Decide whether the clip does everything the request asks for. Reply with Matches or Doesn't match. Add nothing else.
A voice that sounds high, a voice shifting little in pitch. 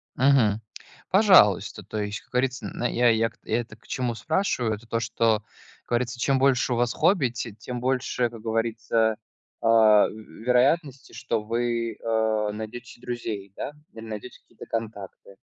Doesn't match